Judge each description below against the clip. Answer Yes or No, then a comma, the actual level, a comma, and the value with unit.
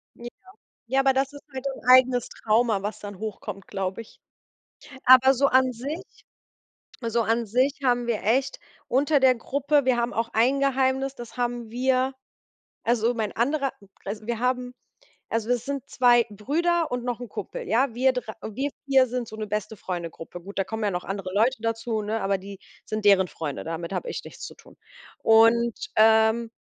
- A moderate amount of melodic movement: Yes, average, 3.3 semitones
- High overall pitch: Yes, high, 235 Hz